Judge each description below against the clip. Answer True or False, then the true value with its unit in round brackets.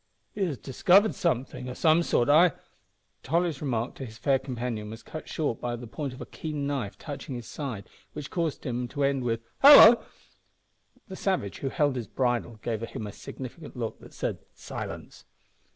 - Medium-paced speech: True (185 wpm)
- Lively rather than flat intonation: False (4.6 semitones)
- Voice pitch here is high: False (130 Hz)